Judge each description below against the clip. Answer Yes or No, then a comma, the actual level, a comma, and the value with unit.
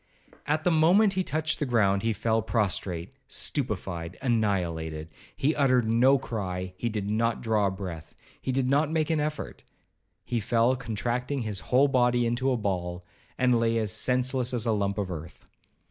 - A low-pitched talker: Yes, low, 115 Hz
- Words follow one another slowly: No, average, 160 wpm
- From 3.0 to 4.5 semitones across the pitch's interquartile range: No, average, 4.9 semitones